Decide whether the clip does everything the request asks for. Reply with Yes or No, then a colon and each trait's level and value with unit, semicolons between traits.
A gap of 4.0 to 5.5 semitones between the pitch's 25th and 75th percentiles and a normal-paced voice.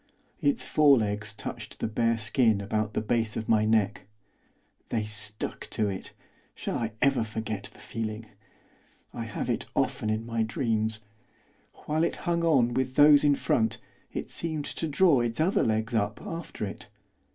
Yes: average, 4.3 semitones; average, 165 wpm